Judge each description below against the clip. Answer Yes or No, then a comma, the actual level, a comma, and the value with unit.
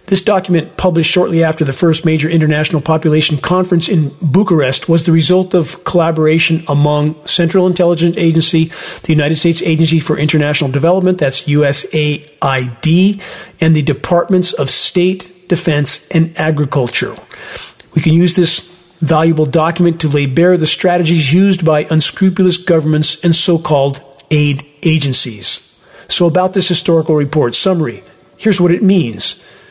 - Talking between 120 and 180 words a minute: Yes, average, 140 wpm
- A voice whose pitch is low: No, medium, 165 Hz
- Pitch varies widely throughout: No, average, 2.7 semitones